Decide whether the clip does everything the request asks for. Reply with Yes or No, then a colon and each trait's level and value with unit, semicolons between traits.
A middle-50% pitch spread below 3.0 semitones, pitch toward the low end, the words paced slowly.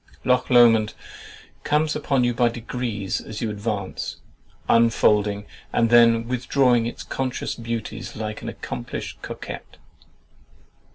Yes: narrow, 2.4 semitones; low, 115 Hz; slow, 115 wpm